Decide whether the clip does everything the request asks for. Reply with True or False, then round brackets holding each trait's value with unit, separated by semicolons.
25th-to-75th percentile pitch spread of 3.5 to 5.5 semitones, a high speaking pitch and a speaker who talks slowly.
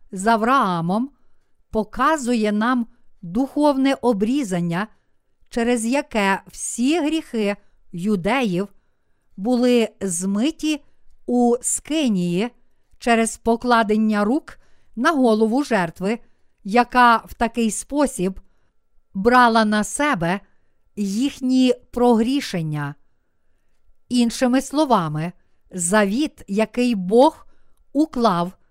True (4.3 semitones; 230 Hz; 75 wpm)